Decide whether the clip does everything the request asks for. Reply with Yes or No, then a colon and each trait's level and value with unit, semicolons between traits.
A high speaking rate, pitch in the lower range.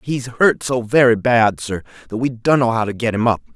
Yes: fast, 235 wpm; low, 120 Hz